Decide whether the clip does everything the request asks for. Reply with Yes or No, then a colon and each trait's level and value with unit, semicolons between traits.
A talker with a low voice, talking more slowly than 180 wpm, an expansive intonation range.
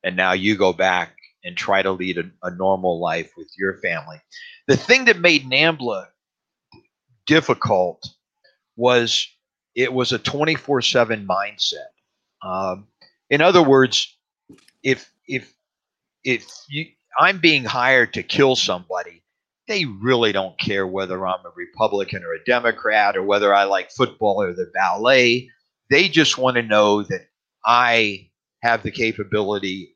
Yes: low, 120 Hz; average, 140 wpm; wide, 6.0 semitones